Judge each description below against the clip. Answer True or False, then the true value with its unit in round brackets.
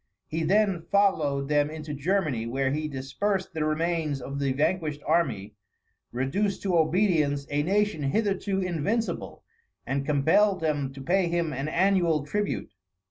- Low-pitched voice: False (155 Hz)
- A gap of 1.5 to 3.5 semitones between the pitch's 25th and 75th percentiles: False (5.0 semitones)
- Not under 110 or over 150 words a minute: True (140 wpm)